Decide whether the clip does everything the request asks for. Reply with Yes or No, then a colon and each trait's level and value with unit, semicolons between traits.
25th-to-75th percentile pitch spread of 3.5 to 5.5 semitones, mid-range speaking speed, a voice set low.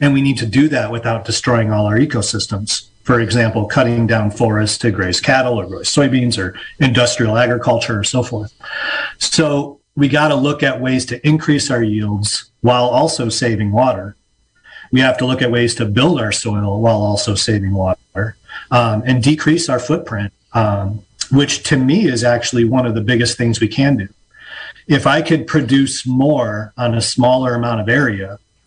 Yes: average, 4.1 semitones; average, 180 wpm; low, 120 Hz